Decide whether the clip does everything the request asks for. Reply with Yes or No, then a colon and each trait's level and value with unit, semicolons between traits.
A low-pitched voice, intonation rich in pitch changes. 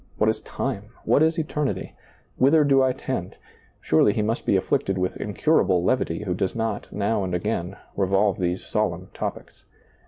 Yes: low, 105 Hz; wide, 5.8 semitones